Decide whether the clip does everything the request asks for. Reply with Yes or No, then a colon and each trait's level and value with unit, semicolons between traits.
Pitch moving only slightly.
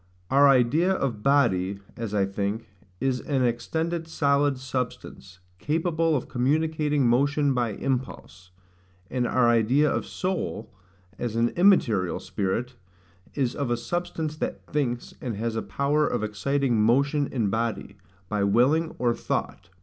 No: average, 4.4 semitones